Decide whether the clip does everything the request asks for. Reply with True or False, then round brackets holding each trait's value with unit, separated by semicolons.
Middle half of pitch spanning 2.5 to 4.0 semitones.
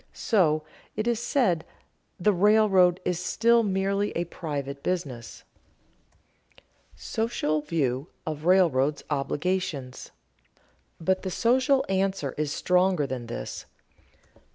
False (5.0 semitones)